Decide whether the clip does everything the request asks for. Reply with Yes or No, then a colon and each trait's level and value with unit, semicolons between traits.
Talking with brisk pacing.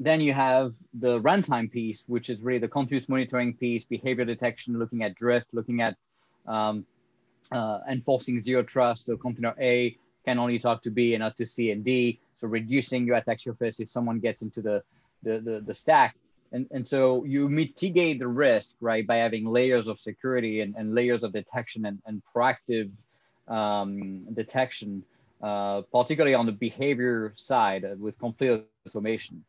No: average, 175 wpm